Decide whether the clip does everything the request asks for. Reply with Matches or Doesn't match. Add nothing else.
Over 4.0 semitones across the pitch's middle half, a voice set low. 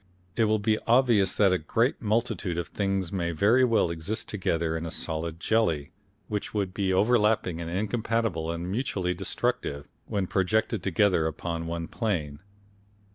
Matches